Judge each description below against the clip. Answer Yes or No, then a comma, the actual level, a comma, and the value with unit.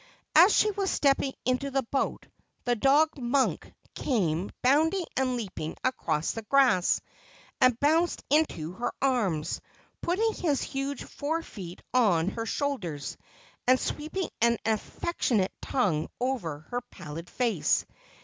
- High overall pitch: Yes, very high, 255 Hz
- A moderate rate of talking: No, slow, 130 wpm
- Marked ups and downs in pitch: Yes, wide, 6.8 semitones